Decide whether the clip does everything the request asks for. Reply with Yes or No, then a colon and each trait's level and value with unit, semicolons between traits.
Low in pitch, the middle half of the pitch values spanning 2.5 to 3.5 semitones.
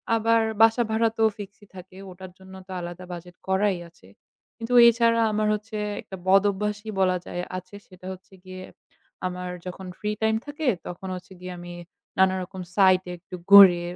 No: high, 190 Hz; average, 2.8 semitones